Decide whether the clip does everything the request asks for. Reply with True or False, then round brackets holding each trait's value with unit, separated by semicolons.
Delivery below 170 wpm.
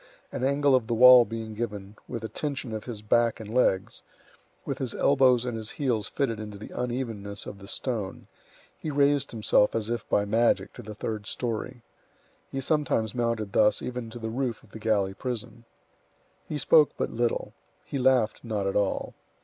False (185 wpm)